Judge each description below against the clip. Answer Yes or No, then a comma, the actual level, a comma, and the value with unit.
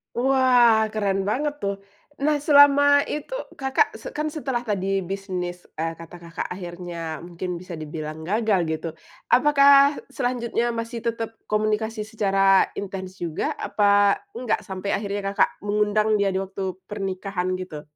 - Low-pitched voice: No, high, 205 Hz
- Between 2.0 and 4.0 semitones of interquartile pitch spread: No, average, 4.5 semitones